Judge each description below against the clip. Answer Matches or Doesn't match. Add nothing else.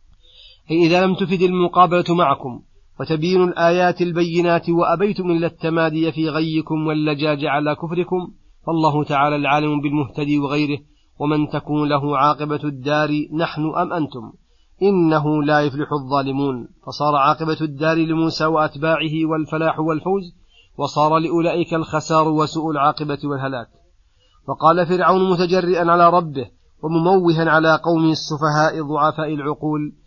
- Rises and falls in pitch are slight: Matches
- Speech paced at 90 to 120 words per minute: Matches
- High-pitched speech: Doesn't match